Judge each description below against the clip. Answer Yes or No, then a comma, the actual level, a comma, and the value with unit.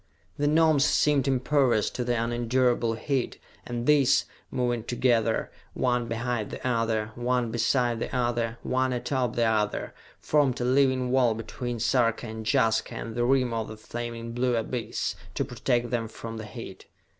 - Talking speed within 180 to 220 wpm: No, average, 160 wpm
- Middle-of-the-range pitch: No, low, 120 Hz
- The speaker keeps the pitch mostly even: Yes, narrow, 1.9 semitones